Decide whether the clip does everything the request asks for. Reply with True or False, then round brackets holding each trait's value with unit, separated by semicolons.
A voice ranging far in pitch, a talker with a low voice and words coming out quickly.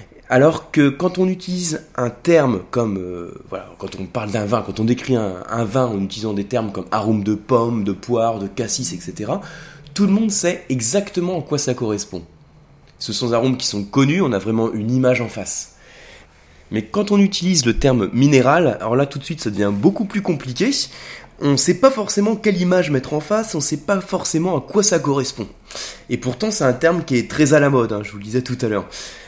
True (7.3 semitones; 130 Hz; 230 wpm)